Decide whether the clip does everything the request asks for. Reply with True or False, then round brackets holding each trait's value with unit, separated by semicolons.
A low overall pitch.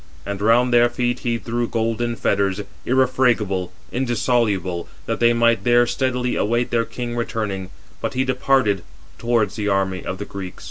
True (115 Hz)